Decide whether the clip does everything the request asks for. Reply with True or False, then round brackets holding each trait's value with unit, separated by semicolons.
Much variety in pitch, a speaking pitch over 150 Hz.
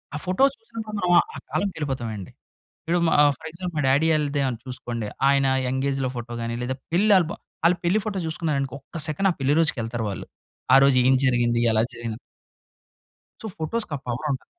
False (5.7 semitones; 140 Hz)